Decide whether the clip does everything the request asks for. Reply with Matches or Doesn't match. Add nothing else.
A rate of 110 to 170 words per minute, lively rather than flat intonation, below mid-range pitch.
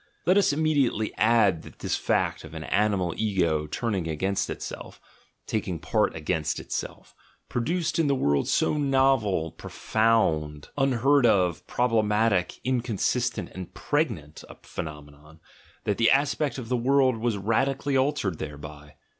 Matches